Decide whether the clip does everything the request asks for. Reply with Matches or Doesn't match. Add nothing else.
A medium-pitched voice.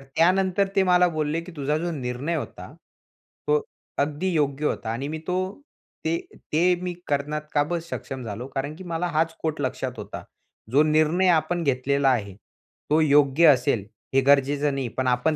Matches